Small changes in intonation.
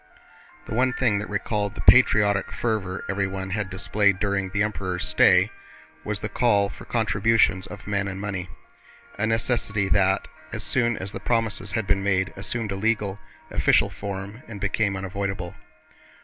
Yes: narrow, 1.7 semitones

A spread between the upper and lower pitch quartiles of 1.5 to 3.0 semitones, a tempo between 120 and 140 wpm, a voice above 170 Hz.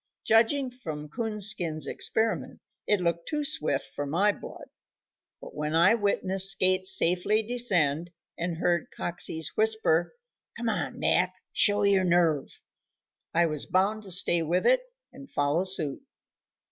No: average, 4.7 semitones; slow, 135 wpm; medium, 185 Hz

